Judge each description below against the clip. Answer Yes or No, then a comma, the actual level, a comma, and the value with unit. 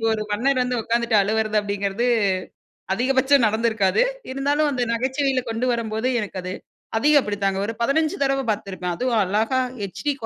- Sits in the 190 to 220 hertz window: No, high, 230 Hz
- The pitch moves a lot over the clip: No, average, 4.1 semitones